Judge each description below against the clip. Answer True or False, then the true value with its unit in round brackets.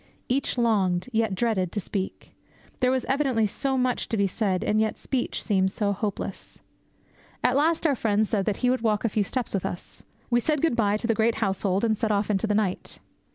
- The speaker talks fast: True (215 wpm)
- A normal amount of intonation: True (3.5 semitones)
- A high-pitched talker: True (220 Hz)